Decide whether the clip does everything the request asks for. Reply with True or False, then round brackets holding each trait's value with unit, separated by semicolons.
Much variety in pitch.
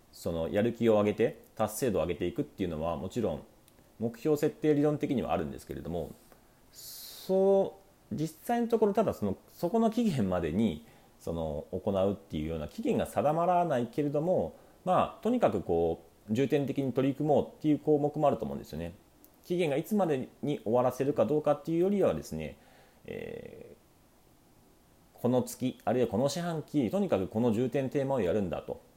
True (7.9 semitones)